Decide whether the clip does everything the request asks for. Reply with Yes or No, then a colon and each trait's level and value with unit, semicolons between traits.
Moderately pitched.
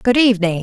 No: high, 215 Hz